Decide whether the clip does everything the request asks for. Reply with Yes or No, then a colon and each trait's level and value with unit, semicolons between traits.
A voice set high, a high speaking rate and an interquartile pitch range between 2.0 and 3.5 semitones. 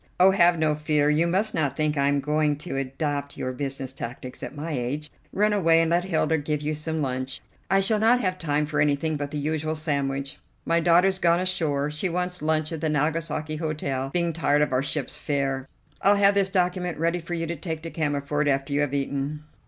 No: medium, 155 Hz; fast, 215 wpm; average, 3.0 semitones